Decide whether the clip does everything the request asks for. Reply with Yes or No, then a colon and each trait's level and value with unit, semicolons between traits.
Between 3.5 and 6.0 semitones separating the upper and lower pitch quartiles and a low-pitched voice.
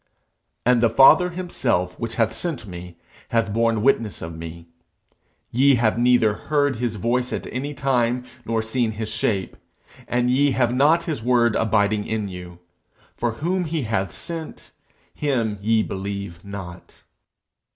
Yes: average, 4.1 semitones; low, 115 Hz